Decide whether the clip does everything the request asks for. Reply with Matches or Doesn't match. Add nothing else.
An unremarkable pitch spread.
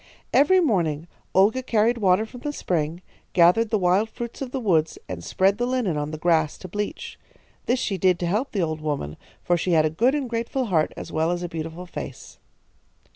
Doesn't match